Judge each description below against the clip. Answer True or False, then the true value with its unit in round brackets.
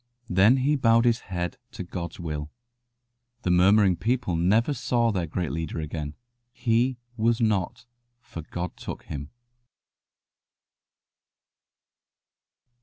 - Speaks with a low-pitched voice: True (95 Hz)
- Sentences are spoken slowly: True (110 wpm)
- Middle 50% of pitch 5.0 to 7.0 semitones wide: True (5.4 semitones)